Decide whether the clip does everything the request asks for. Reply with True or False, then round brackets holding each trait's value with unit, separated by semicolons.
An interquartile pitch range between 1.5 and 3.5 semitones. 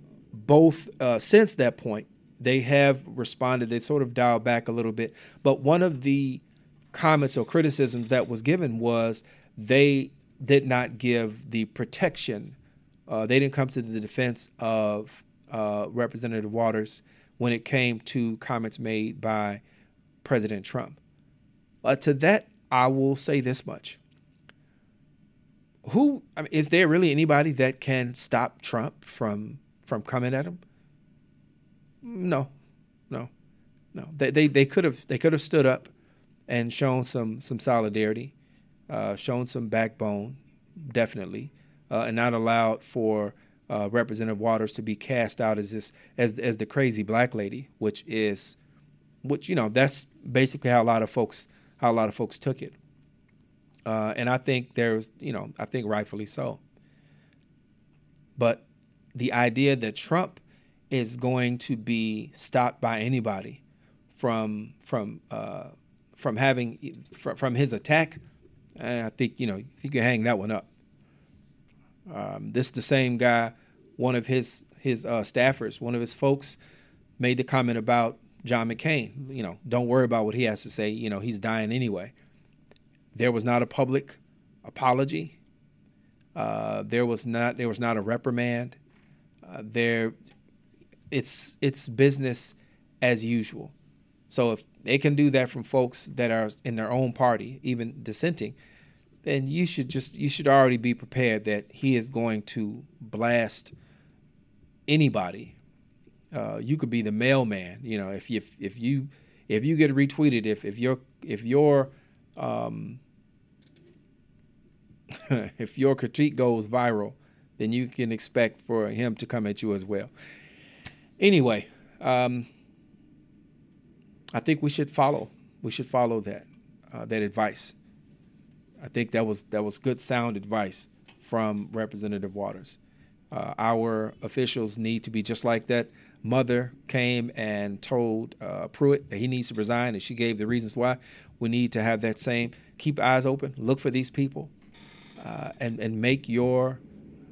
True (3.2 semitones)